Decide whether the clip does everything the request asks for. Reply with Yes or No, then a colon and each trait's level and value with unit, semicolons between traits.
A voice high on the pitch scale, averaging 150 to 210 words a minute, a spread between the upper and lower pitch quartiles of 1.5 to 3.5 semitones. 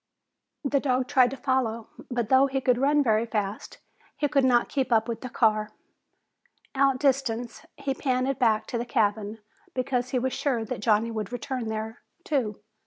Yes: high, 245 Hz; average, 175 wpm; average, 3.1 semitones